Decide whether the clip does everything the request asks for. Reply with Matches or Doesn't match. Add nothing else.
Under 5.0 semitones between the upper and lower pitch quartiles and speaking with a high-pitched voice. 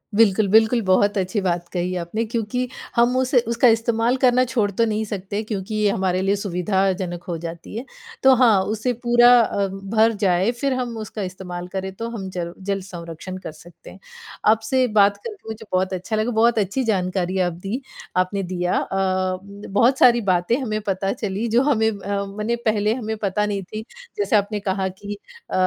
Matches